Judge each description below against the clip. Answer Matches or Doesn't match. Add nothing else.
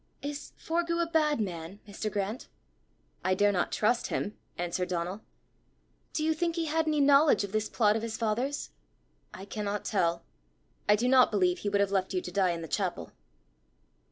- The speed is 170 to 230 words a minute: Matches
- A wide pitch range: Matches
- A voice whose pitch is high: Matches